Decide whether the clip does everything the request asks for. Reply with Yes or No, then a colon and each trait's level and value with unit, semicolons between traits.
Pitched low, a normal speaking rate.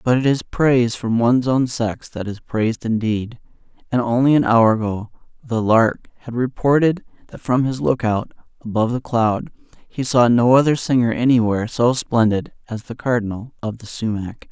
Yes: low, 120 Hz; average, 170 wpm